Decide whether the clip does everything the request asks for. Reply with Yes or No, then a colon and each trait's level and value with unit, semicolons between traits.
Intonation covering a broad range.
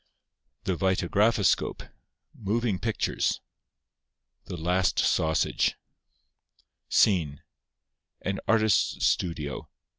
No: average, 4.1 semitones